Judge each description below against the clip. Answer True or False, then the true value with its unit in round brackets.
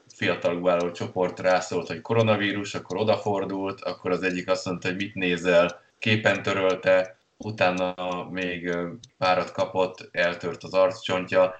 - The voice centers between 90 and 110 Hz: True (95 Hz)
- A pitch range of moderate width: False (1.3 semitones)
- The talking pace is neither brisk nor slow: True (130 wpm)